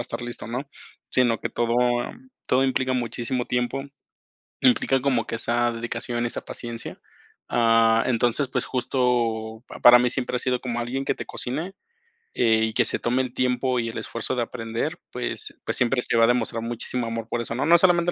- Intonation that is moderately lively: No, narrow, 1.7 semitones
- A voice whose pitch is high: No, low, 120 Hz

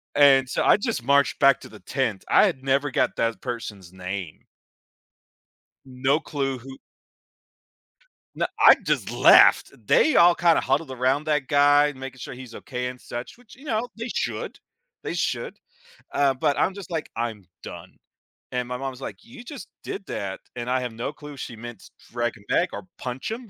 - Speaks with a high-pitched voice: No, low, 135 Hz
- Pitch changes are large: No, average, 3.6 semitones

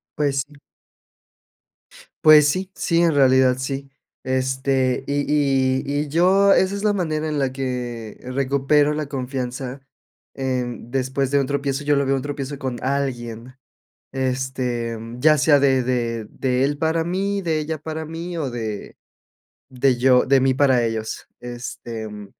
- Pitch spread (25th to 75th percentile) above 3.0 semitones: No, average, 2.7 semitones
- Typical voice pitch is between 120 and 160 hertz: Yes, low, 135 Hz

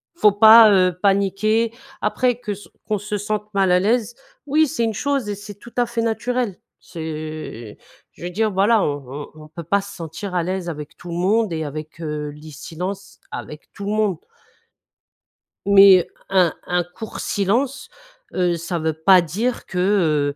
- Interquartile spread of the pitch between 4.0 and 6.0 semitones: Yes, average, 4.4 semitones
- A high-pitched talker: Yes, high, 195 Hz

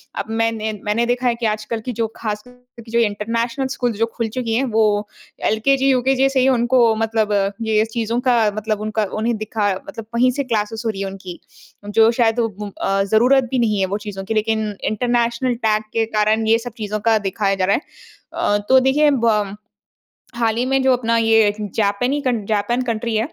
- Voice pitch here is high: Yes, high, 225 Hz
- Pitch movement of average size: No, narrow, 2.3 semitones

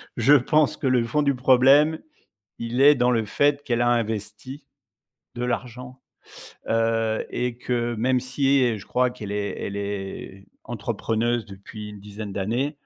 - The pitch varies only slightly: No, average, 3.0 semitones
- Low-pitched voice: Yes, low, 120 Hz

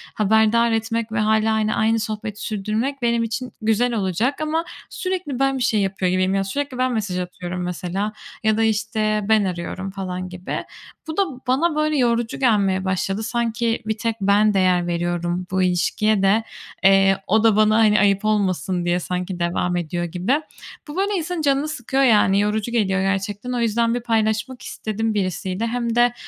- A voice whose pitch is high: Yes, high, 215 Hz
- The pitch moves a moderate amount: Yes, average, 3.6 semitones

